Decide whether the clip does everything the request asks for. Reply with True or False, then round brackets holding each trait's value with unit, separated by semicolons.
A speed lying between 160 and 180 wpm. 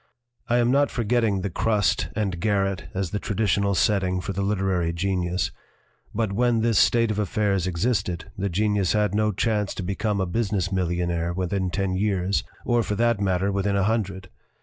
True (175 wpm)